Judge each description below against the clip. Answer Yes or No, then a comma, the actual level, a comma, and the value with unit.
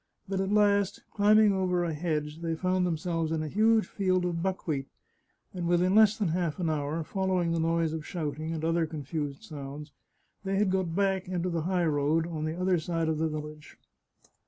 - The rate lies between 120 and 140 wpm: No, average, 195 wpm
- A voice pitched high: No, medium, 170 Hz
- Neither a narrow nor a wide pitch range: Yes, average, 3.1 semitones